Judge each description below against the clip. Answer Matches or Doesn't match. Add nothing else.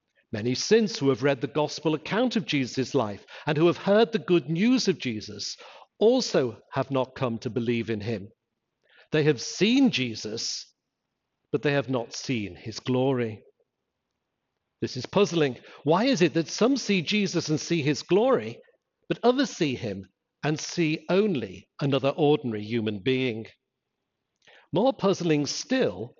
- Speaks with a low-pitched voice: Doesn't match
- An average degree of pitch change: Doesn't match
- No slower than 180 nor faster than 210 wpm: Doesn't match